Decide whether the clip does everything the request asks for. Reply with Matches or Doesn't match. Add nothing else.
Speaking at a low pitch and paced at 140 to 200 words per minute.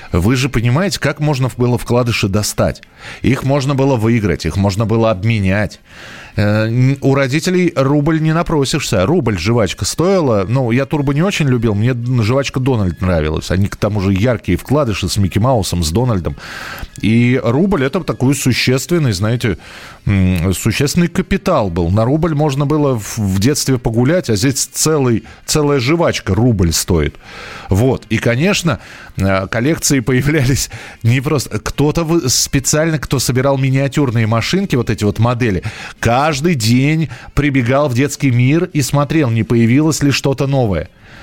Matches